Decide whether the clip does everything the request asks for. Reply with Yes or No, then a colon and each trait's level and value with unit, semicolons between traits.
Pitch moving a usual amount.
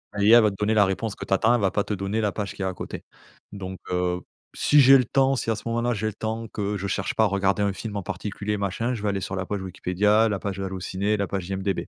No: narrow, 2.3 semitones